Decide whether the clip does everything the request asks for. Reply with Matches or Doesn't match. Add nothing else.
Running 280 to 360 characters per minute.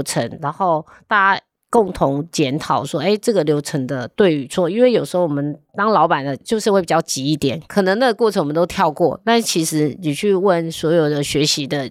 Matches